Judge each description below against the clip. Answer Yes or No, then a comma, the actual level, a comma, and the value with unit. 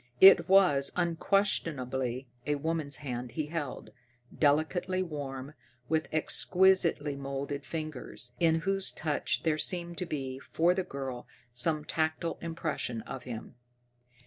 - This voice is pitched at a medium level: Yes, medium, 155 Hz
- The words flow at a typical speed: No, slow, 120 wpm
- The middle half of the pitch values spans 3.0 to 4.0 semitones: Yes, average, 3.7 semitones